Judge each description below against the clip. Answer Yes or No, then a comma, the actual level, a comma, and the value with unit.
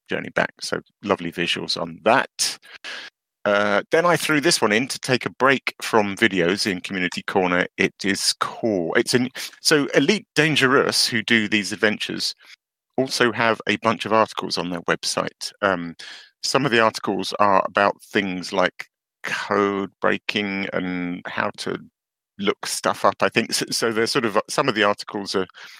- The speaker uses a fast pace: No, average, 170 wpm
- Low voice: Yes, low, 105 Hz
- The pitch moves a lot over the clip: No, average, 3.1 semitones